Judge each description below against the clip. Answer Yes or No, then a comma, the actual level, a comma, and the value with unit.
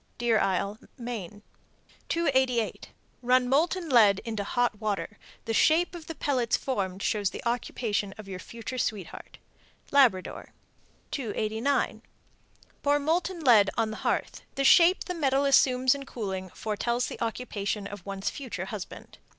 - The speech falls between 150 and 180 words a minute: No, average, 140 wpm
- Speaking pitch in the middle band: No, high, 235 Hz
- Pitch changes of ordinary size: Yes, average, 4.9 semitones